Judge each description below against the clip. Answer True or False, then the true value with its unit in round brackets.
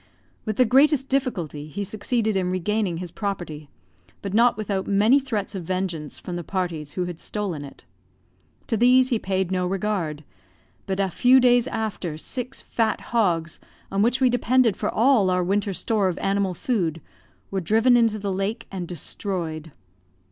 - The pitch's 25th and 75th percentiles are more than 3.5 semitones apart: True (4.3 semitones)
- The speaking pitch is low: False (195 Hz)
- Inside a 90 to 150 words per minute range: False (170 wpm)